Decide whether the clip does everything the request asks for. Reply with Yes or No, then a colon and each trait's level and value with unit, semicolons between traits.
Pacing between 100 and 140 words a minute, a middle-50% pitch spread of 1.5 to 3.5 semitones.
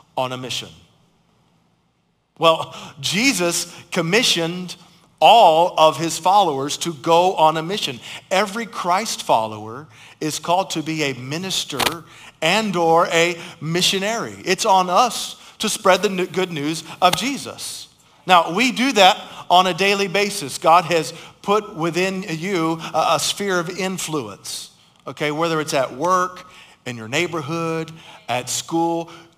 Yes: slow, 135 wpm; average, 3.0 semitones